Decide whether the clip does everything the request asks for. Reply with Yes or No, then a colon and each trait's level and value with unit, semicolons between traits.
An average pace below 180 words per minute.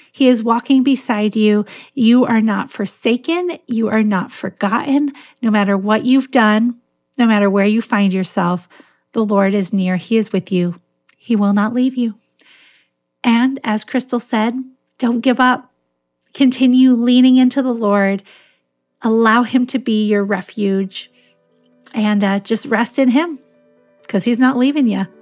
Yes: average, 155 wpm